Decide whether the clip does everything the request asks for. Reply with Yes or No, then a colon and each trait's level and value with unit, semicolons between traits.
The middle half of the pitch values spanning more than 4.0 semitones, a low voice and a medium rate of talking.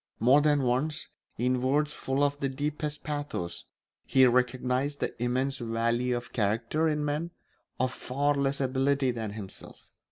No: average, 2.8 semitones; low, 130 Hz; average, 150 wpm